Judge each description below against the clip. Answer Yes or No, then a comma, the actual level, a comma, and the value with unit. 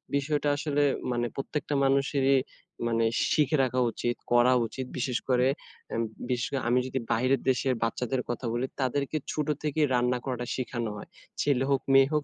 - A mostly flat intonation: Yes, narrow, 2.3 semitones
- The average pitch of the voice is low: Yes, low, 130 Hz